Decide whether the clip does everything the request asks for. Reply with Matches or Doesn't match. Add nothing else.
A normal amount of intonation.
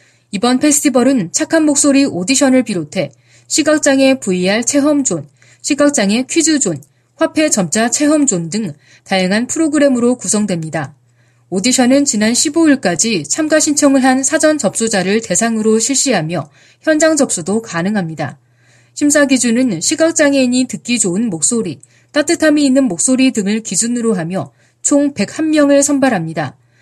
Doesn't match